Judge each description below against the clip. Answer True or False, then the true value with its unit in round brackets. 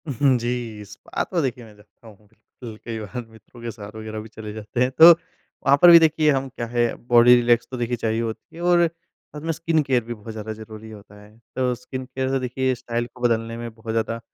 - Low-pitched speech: True (120 Hz)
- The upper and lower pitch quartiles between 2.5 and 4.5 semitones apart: True (2.9 semitones)